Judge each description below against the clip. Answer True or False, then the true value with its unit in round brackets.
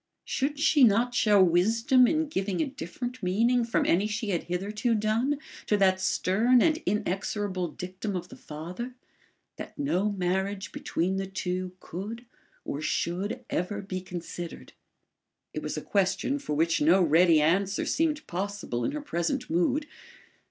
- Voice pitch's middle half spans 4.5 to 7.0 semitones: True (5.0 semitones)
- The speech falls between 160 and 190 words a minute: False (150 wpm)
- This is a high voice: True (200 Hz)